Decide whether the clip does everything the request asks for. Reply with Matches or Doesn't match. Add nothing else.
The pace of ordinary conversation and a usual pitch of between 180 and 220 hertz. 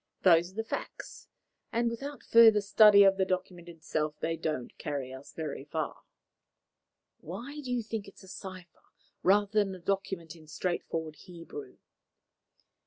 Matches